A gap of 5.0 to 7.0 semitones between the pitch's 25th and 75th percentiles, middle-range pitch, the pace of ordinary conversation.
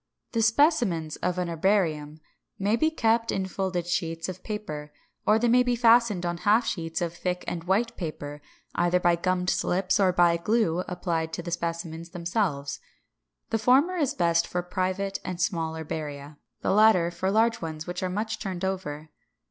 No: average, 4.2 semitones; medium, 180 Hz; average, 175 wpm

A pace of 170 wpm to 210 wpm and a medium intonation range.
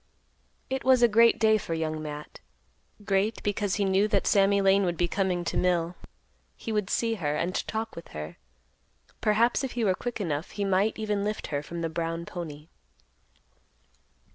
Yes: average, 180 wpm; average, 4.3 semitones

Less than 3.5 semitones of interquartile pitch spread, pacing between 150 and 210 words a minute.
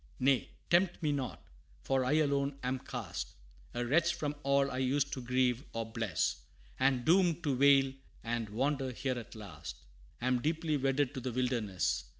Yes: average, 2.9 semitones; average, 165 wpm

